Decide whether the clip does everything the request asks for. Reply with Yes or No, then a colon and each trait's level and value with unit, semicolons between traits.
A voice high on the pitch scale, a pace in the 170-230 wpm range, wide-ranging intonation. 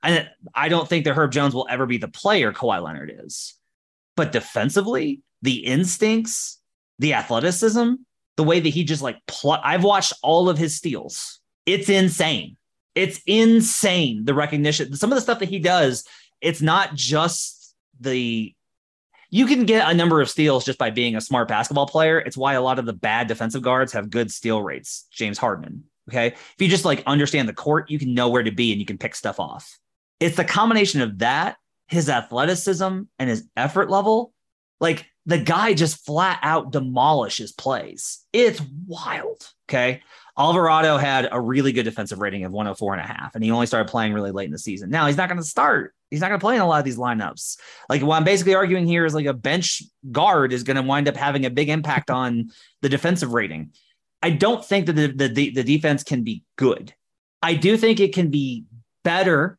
No: medium, 150 Hz; average, 200 wpm; wide, 6.2 semitones